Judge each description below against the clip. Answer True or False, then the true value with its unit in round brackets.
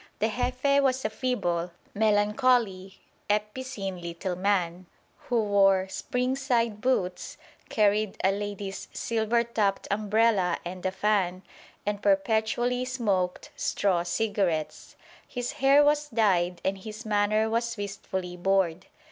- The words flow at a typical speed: False (120 wpm)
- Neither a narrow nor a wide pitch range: True (3.6 semitones)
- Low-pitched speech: False (205 Hz)